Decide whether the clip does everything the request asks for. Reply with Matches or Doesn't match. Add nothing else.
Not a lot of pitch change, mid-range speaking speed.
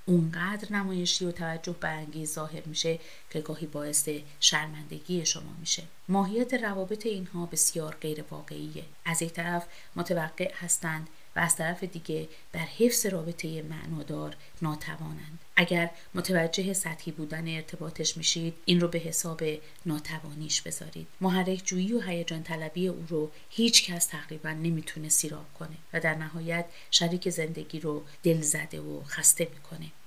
Matches